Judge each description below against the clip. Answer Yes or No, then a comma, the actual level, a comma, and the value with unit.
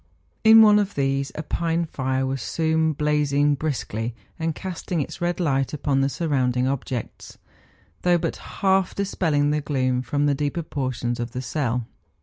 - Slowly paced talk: No, average, 165 wpm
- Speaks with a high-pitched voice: No, medium, 145 Hz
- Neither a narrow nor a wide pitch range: Yes, average, 3.7 semitones